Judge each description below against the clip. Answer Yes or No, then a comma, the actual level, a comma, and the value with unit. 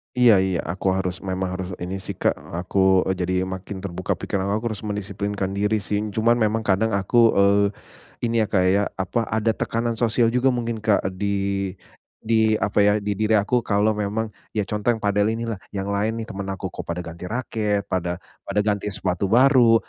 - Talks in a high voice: No, low, 105 Hz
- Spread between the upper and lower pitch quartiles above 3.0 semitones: No, narrow, 2.6 semitones